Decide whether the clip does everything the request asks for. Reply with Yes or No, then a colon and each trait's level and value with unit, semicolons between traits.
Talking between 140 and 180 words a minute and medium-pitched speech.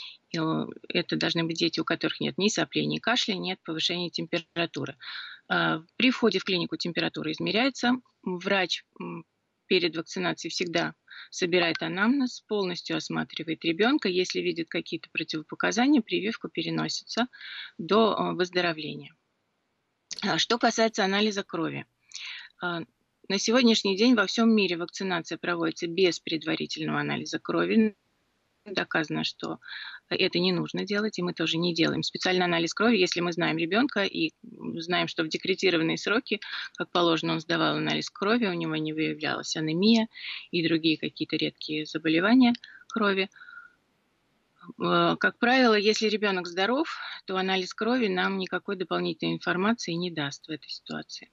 No: average, 130 wpm; medium, 180 Hz